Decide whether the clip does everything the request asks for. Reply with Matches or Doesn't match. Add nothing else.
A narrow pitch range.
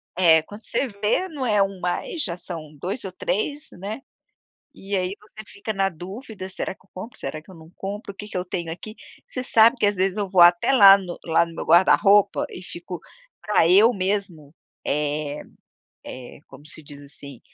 Doesn't match